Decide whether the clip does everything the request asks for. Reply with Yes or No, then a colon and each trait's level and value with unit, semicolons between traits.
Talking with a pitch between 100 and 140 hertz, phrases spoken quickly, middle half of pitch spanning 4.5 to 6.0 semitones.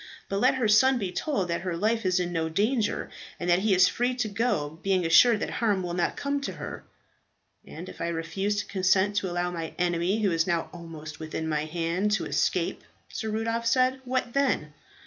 No: high, 190 Hz; fast, 210 wpm; average, 5.0 semitones